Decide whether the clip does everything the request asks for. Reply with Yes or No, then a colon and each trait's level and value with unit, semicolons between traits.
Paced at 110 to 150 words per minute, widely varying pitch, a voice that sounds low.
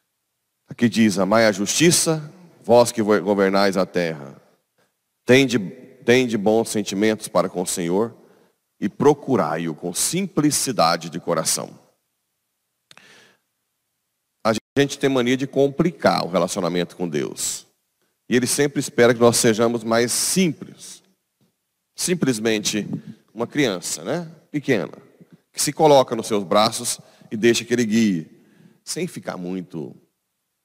Yes: slow, 120 wpm; wide, 5.7 semitones; low, 115 Hz